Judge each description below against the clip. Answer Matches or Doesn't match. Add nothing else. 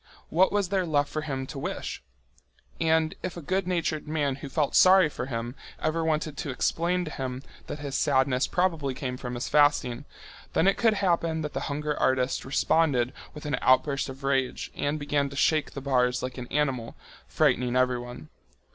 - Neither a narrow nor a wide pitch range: Matches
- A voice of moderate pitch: Matches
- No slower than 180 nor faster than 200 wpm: Matches